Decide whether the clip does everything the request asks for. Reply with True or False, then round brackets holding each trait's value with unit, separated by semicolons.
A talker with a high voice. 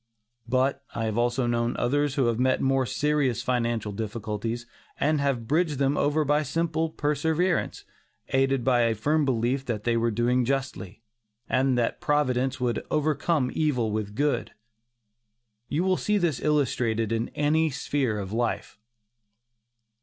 False (130 Hz)